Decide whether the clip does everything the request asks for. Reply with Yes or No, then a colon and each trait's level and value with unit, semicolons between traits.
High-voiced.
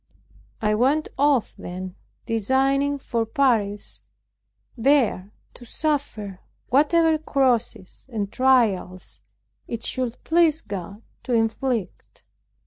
Yes: high, 240 Hz